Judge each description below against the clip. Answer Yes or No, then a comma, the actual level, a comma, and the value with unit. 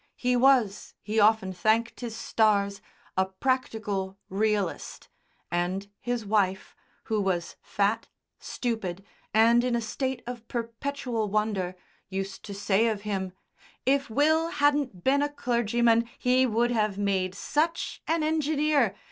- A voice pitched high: Yes, high, 225 Hz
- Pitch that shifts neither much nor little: Yes, average, 4.1 semitones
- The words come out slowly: Yes, slow, 130 wpm